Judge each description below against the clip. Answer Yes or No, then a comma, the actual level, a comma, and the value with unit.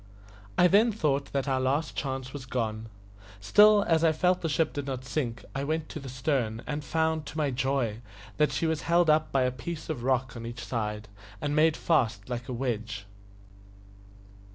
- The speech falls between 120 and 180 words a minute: No, average, 195 wpm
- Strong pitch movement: No, average, 4.3 semitones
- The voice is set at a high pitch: No, low, 135 Hz